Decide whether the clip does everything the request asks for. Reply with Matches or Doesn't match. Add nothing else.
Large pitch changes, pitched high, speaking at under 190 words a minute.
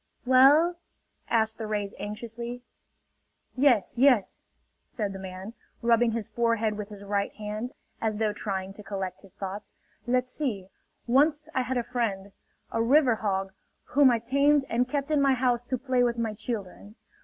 Doesn't match